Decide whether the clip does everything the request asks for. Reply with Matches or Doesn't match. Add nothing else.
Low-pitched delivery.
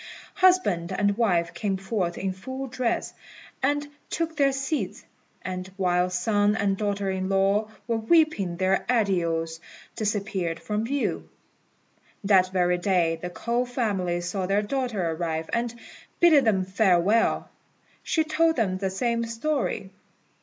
Doesn't match